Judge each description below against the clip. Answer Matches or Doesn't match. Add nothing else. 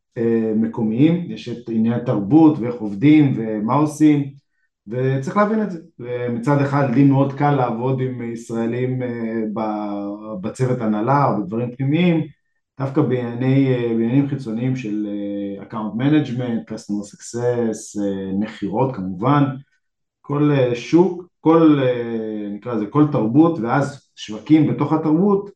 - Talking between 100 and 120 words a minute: Matches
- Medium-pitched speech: Doesn't match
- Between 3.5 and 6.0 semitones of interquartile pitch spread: Matches